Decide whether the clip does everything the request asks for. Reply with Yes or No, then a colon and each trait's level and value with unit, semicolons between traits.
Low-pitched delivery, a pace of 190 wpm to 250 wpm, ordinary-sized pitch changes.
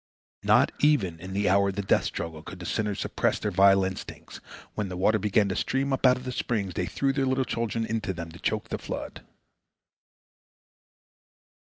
Yes: low, 100 Hz; average, 195 wpm; average, 4.1 semitones